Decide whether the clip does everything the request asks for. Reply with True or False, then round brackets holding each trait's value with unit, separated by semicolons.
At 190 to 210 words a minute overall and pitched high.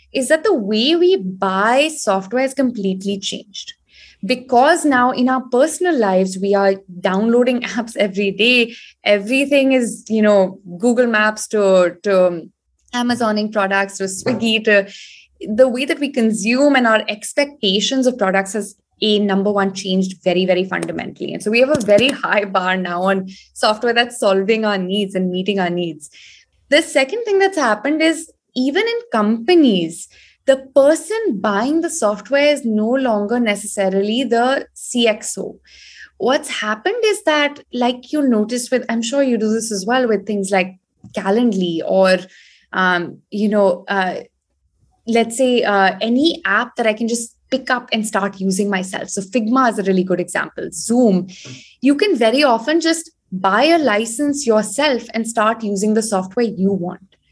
False (160 wpm; 220 Hz)